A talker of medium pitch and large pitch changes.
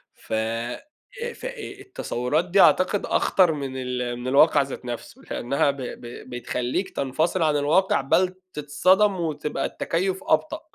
Yes: medium, 150 Hz; wide, 6.7 semitones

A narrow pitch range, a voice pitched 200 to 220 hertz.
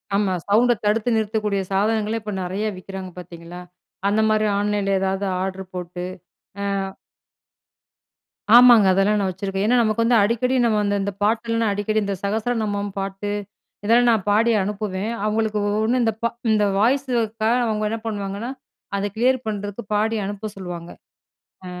Yes: narrow, 2.3 semitones; high, 210 Hz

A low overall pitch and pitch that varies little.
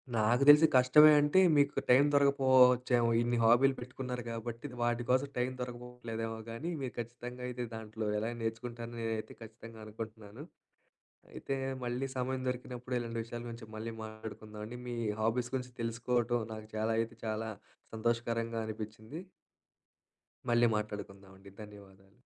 Yes: low, 120 Hz; narrow, 2.0 semitones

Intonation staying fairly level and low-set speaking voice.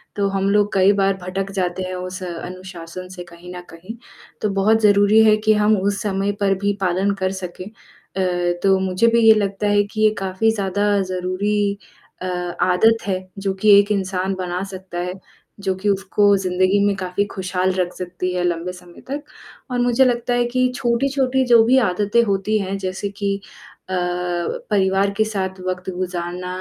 No: narrow, 2.2 semitones; high, 195 Hz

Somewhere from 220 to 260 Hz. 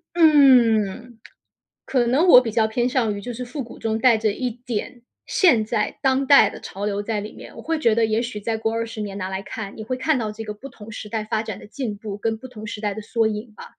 Yes: high, 225 Hz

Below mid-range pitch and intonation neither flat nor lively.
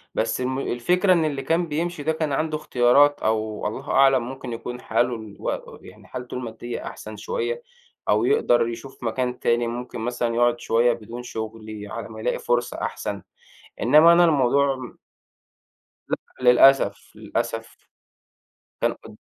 Yes: low, 125 Hz; average, 3.7 semitones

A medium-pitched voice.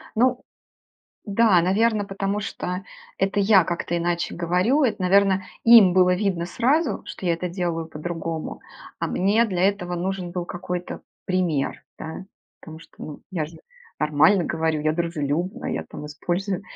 Yes: medium, 180 Hz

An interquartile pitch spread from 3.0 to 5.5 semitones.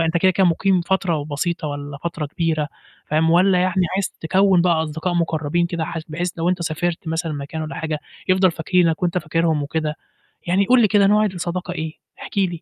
No: narrow, 2.5 semitones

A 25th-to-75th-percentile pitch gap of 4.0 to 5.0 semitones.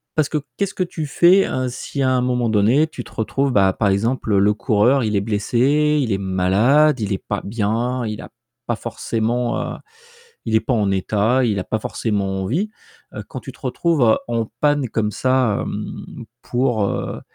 Yes: average, 4.4 semitones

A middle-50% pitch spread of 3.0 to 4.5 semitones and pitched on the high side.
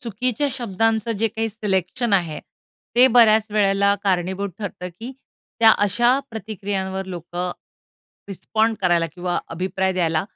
Yes: average, 3.5 semitones; high, 200 Hz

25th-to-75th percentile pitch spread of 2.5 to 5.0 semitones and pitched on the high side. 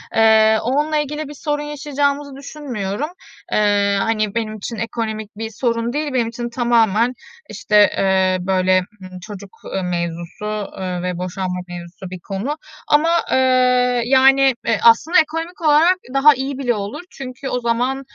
No: wide, 5.6 semitones; high, 230 Hz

